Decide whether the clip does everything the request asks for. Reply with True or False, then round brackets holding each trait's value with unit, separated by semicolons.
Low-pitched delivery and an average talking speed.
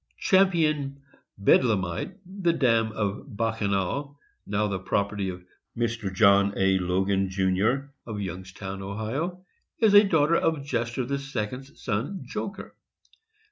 False (110 Hz; 120 wpm)